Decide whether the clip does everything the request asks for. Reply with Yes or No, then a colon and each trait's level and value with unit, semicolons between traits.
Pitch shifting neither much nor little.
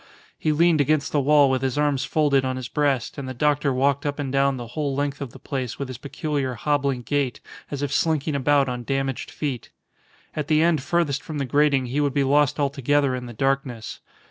No: narrow, 2.0 semitones